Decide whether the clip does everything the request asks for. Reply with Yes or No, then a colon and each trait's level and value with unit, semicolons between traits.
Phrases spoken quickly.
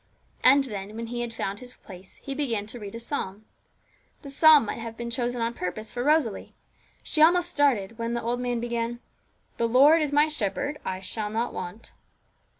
No: average, 195 wpm